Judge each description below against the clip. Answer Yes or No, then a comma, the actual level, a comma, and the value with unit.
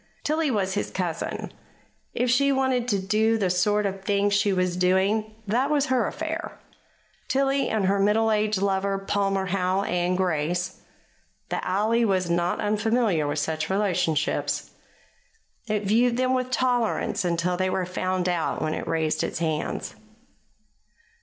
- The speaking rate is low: No, average, 150 wpm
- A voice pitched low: No, high, 200 Hz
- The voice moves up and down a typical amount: Yes, average, 3.7 semitones